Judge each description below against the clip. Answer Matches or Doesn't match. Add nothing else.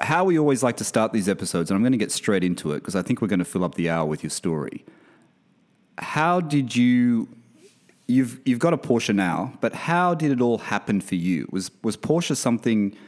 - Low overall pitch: Matches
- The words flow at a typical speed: Doesn't match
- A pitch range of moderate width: Doesn't match